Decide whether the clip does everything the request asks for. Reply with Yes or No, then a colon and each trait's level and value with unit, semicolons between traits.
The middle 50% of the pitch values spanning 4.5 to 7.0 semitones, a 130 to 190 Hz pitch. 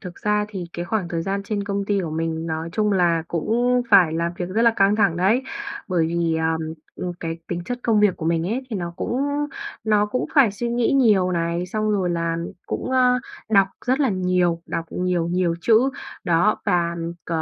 No: average, 4.0 semitones; medium, 185 Hz